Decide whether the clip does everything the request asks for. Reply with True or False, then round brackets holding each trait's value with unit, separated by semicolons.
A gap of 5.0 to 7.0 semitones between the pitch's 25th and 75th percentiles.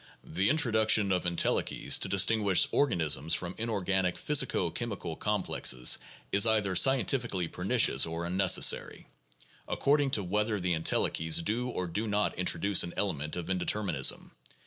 False (4.1 semitones)